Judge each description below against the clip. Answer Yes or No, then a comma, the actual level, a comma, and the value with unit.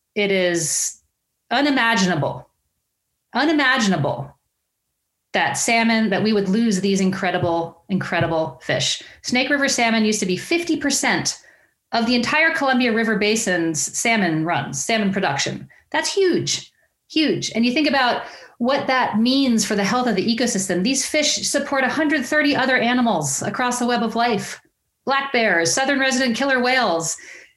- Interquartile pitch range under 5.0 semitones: No, wide, 5.5 semitones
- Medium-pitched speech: No, high, 235 Hz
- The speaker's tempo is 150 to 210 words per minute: No, average, 140 wpm